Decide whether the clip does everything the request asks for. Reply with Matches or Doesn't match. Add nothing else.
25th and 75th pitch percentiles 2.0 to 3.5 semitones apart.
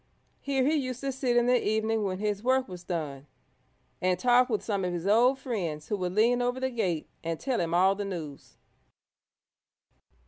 Doesn't match